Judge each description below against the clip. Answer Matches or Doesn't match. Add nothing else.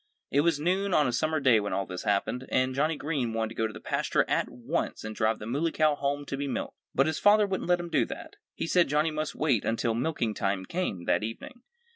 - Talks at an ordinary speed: Doesn't match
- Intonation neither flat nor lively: Doesn't match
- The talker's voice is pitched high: Doesn't match